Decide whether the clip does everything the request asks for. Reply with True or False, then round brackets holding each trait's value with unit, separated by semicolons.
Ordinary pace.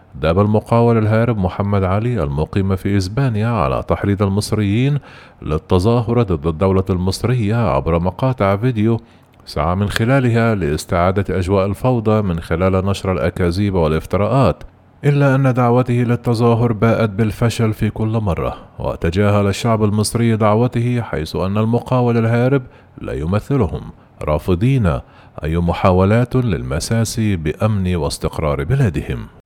True (110 wpm)